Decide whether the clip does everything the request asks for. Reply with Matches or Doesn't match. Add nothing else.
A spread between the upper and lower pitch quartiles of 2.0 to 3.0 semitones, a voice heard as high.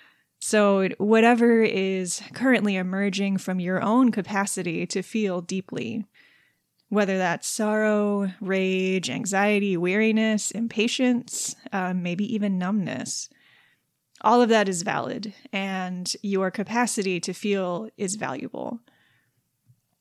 Matches